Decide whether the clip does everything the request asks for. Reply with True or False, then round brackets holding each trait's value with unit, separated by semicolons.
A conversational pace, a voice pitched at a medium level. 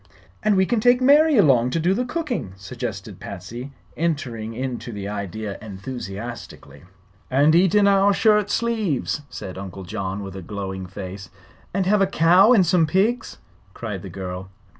False (160 wpm; 130 Hz)